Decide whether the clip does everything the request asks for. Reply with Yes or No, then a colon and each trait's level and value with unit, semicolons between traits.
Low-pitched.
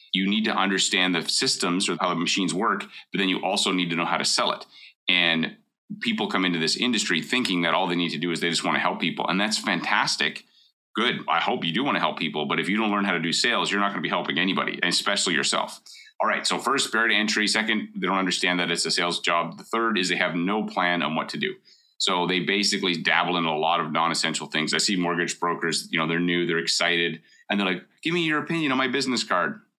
Yes: very low, 90 Hz